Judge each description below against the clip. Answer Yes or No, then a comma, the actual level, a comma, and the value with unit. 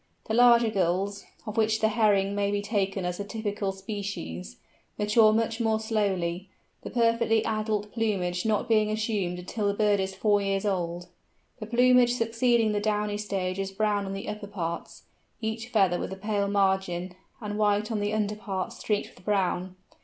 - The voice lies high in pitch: Yes, high, 205 Hz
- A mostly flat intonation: Yes, narrow, 2.2 semitones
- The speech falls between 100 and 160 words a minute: No, average, 175 wpm